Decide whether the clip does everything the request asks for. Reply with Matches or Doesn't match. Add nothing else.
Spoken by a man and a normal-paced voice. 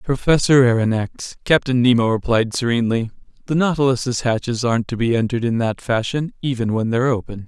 Matches